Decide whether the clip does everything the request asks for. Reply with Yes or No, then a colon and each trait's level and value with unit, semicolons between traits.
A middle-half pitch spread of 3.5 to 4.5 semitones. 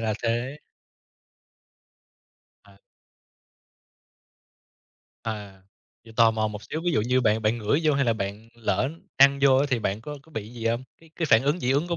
Yes: average, 4.2 semitones